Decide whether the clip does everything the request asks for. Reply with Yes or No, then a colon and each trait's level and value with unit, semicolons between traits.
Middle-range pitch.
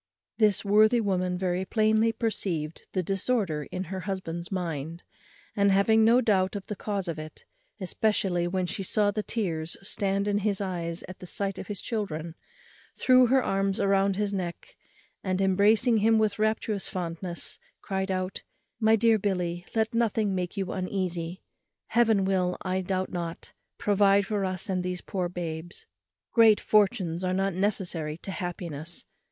No: high, 195 Hz